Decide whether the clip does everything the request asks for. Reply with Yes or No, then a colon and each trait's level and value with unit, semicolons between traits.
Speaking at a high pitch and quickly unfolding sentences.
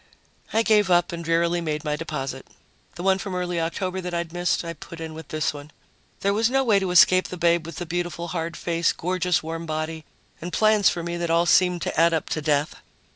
No: medium, 170 Hz; fast, 230 wpm